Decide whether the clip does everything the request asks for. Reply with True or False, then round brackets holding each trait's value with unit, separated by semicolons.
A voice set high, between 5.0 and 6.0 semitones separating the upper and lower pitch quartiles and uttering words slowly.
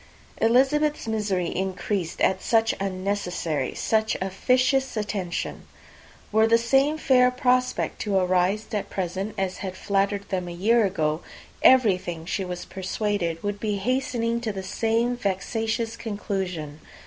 False (205 Hz; 3.7 semitones; 130 wpm)